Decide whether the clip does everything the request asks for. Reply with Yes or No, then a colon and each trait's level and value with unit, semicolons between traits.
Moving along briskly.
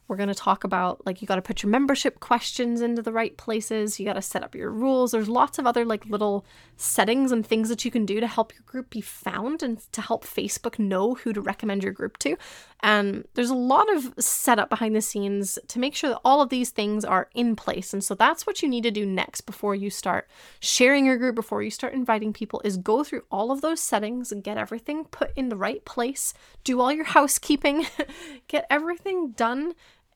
Yes: fast, 225 wpm